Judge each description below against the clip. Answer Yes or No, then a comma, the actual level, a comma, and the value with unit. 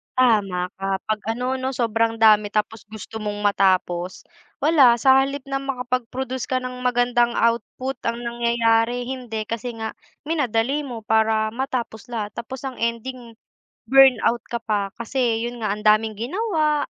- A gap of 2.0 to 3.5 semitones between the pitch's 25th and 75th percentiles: Yes, average, 2.7 semitones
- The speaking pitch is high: Yes, high, 235 Hz